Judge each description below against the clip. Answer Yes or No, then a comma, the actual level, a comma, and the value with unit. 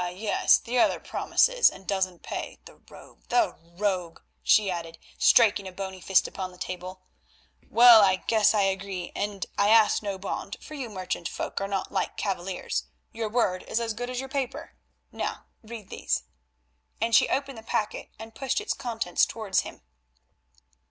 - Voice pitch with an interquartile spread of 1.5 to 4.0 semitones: Yes, average, 3.6 semitones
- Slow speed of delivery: No, average, 165 wpm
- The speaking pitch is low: No, high, 205 Hz